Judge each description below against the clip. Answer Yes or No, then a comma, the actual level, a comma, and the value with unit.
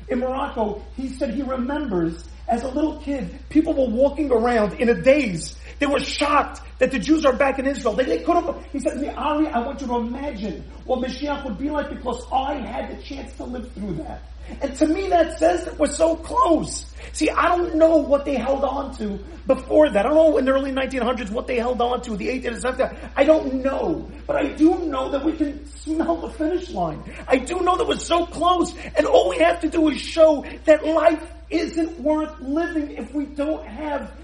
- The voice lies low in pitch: No, very high, 285 Hz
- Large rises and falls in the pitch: No, average, 3.5 semitones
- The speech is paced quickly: Yes, fast, 225 wpm